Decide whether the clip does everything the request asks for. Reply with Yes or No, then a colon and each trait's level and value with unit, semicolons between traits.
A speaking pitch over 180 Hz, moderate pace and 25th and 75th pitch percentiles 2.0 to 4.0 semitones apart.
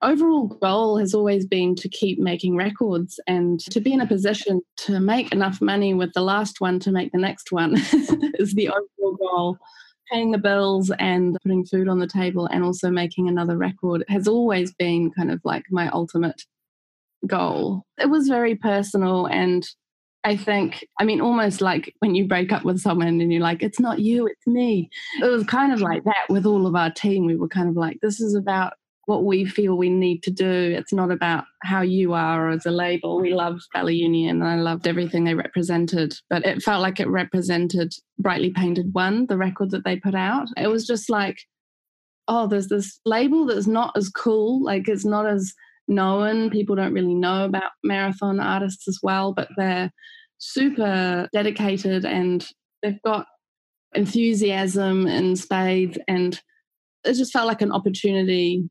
Yes: high, 190 Hz; average, 185 wpm; average, 2.7 semitones